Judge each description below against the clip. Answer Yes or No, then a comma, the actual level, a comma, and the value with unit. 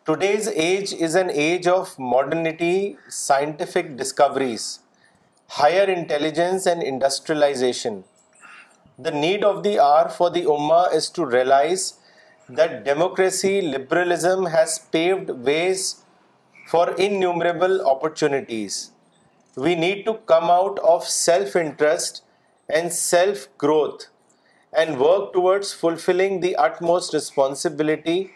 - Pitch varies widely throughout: No, average, 3.5 semitones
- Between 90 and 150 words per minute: Yes, slow, 110 wpm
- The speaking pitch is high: No, medium, 175 Hz